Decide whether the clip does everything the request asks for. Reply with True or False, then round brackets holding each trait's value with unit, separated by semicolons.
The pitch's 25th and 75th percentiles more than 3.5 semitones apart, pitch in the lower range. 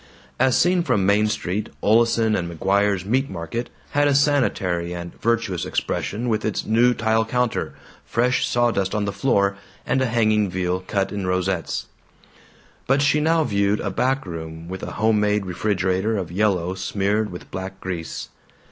True (4.0 semitones; 105 Hz)